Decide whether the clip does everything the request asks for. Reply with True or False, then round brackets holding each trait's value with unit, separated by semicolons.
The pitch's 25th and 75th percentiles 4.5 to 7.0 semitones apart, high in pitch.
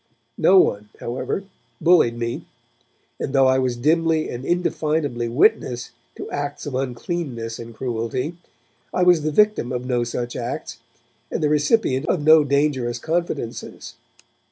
False (4.8 semitones; 135 Hz)